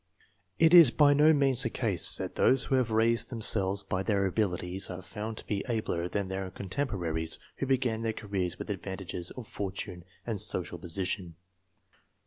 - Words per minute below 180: Yes, average, 170 wpm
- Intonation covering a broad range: No, average, 4.1 semitones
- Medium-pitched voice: No, low, 105 Hz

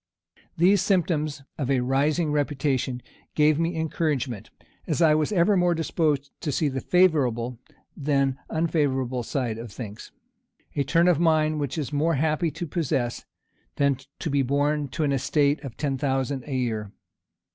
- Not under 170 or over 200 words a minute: No, average, 160 wpm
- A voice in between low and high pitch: Yes, medium, 145 Hz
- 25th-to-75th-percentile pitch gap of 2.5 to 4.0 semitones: Yes, average, 3.2 semitones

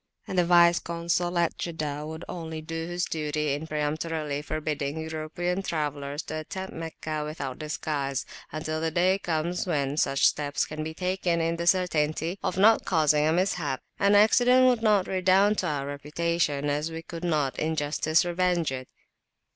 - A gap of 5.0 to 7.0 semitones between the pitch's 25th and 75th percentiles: No, average, 2.7 semitones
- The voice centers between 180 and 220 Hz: No, medium, 160 Hz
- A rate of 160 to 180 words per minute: Yes, average, 170 wpm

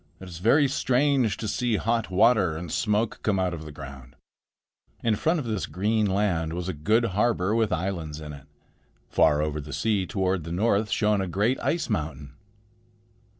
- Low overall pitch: Yes, very low, 95 Hz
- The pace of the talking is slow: No, average, 185 wpm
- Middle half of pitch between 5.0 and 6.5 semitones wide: Yes, wide, 5.6 semitones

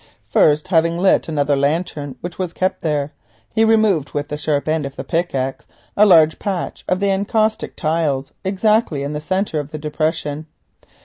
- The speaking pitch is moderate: Yes, medium, 160 Hz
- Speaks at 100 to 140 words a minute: No, average, 175 wpm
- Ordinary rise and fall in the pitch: Yes, average, 4.2 semitones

